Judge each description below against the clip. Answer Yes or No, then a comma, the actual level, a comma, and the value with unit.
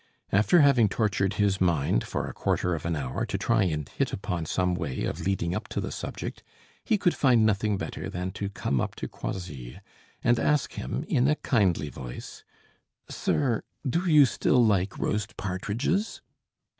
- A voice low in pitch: Yes, low, 100 Hz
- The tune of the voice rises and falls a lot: Yes, wide, 5.7 semitones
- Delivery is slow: No, average, 175 wpm